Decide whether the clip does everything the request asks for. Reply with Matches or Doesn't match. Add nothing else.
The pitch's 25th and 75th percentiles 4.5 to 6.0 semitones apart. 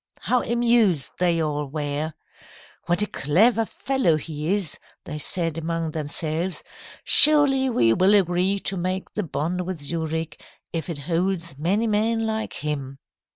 Matches